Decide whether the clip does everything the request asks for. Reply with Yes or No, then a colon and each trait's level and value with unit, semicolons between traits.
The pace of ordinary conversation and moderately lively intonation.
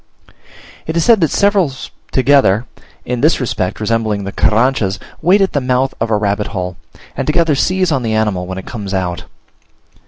No: average, 180 wpm; wide, 7.0 semitones